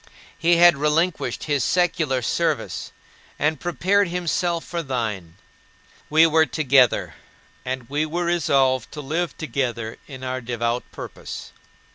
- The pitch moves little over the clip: No, average, 4.9 semitones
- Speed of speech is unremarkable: No, slow, 125 wpm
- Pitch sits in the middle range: Yes, medium, 150 Hz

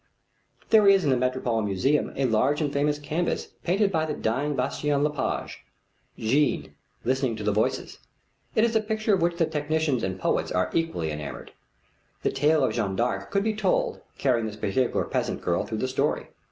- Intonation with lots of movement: Yes, wide, 6.5 semitones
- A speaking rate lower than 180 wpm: No, average, 190 wpm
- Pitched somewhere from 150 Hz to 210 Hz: No, medium, 140 Hz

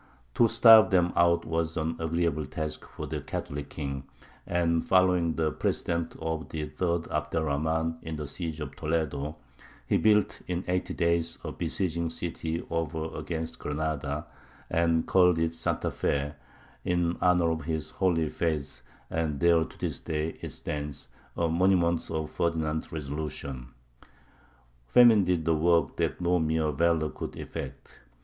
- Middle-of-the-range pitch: No, very low, 80 Hz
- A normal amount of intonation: No, narrow, 1.8 semitones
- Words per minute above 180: No, average, 150 wpm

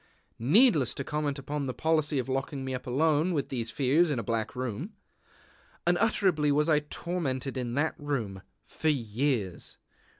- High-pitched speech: No, medium, 140 Hz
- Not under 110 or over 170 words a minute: Yes, average, 160 wpm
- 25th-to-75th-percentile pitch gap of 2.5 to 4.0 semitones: Yes, average, 3.5 semitones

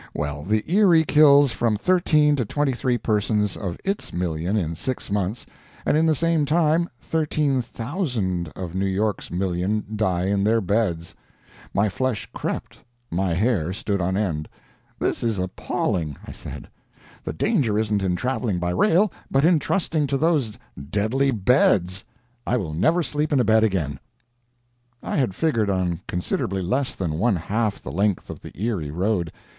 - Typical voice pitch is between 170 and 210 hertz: No, low, 105 Hz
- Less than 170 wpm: Yes, average, 160 wpm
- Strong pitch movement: Yes, wide, 6.9 semitones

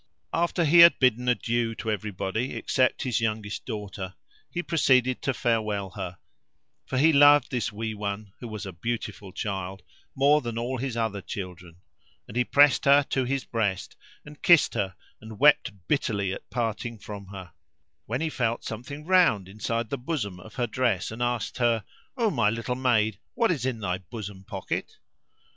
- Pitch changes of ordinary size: Yes, average, 4.2 semitones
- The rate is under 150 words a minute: No, average, 175 wpm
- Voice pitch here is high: No, low, 115 Hz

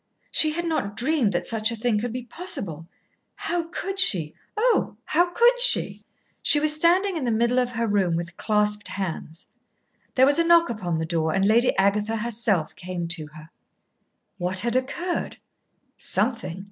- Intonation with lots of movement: Yes, wide, 8.6 semitones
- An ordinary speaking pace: Yes, average, 170 wpm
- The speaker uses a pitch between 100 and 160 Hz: No, high, 230 Hz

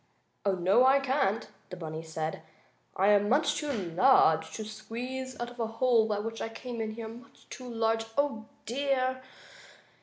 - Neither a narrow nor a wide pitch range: Yes, average, 4.0 semitones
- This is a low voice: No, high, 225 Hz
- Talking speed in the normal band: Yes, average, 175 wpm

